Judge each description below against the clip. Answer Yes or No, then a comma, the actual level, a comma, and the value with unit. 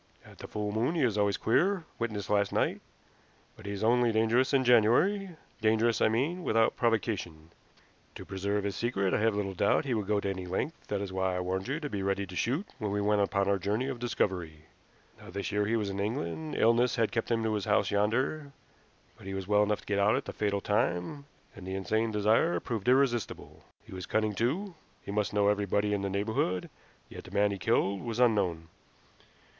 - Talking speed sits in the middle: No, fast, 215 wpm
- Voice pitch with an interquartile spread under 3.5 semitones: Yes, average, 3.0 semitones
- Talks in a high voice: No, low, 105 Hz